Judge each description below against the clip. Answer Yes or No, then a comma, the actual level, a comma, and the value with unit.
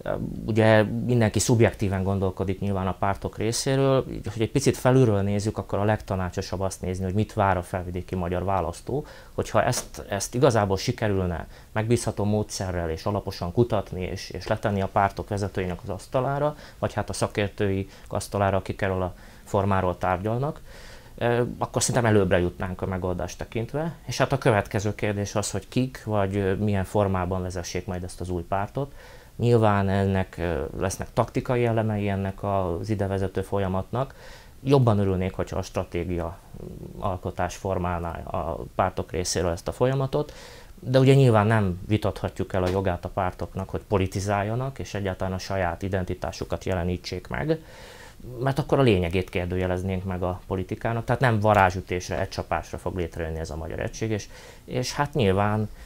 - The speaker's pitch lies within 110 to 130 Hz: No, low, 100 Hz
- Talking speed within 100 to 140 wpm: No, fast, 155 wpm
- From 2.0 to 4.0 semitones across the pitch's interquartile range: Yes, average, 3.4 semitones